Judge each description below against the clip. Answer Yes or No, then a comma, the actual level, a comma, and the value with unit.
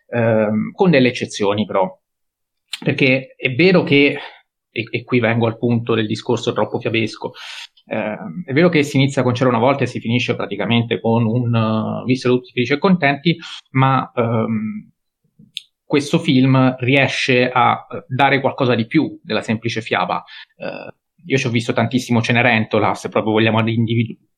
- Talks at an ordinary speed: Yes, average, 160 wpm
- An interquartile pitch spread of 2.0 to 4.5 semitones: Yes, average, 2.9 semitones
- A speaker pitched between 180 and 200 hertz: No, low, 125 Hz